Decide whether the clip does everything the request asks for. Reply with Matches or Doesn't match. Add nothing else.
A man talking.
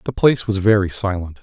Matches